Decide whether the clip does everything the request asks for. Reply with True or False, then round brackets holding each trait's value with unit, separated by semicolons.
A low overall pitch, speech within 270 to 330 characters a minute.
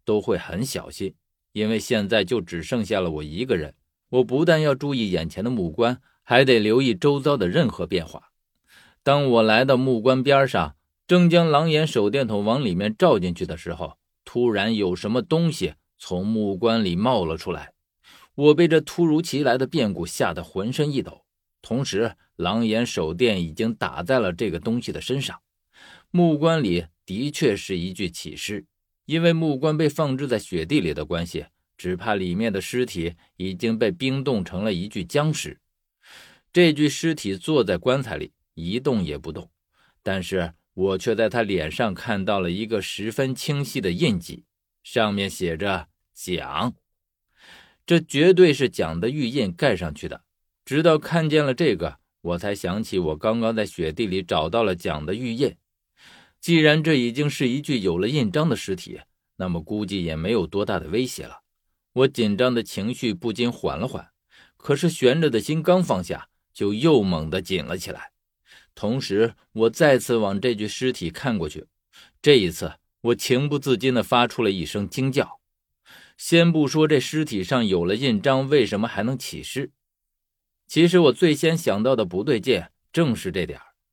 False (120 Hz; 250 characters per minute)